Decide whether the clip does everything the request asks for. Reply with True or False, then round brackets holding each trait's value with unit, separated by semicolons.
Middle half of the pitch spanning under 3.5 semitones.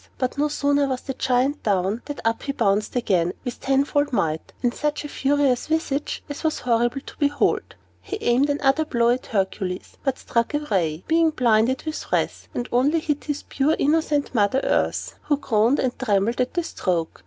False (4.1 semitones)